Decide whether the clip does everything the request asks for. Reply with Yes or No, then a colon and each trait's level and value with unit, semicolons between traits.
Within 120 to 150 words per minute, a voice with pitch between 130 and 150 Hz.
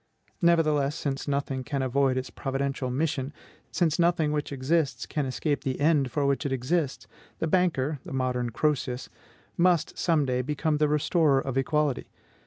No: average, 160 wpm; medium, 140 Hz